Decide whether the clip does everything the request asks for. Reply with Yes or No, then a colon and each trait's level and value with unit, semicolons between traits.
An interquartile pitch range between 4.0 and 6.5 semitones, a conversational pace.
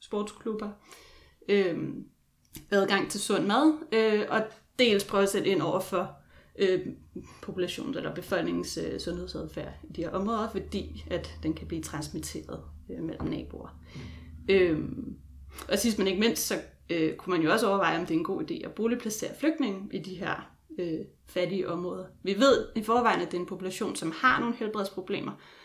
Yes: average, 4.3 semitones; average, 175 wpm